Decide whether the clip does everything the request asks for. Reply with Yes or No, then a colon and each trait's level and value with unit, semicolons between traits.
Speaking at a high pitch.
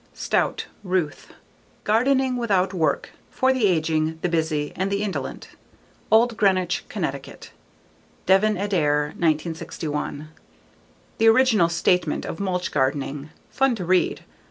No: medium, 180 Hz